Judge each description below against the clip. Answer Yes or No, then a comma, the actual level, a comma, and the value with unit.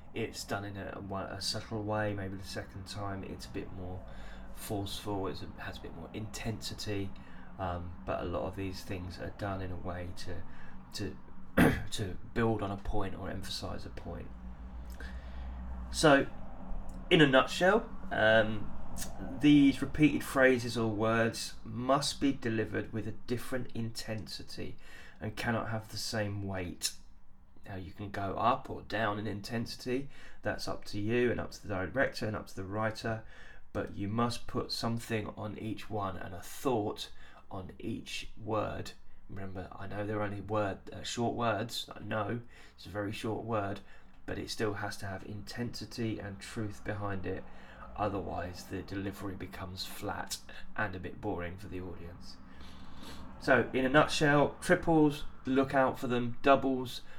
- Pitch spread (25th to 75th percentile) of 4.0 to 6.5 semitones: No, average, 3.3 semitones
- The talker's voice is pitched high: No, low, 100 Hz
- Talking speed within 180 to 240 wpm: No, average, 165 wpm